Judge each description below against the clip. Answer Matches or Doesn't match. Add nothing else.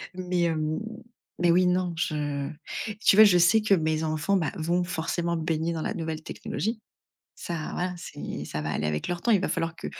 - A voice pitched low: Doesn't match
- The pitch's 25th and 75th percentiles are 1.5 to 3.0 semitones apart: Matches